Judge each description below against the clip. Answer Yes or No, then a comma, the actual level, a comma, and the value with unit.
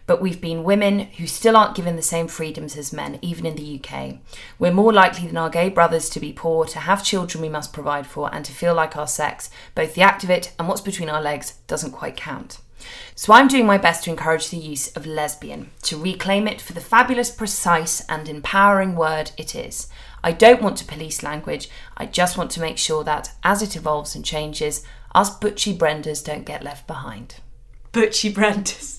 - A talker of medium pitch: Yes, medium, 165 Hz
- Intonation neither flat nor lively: Yes, average, 4.2 semitones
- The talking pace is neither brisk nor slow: No, fast, 215 wpm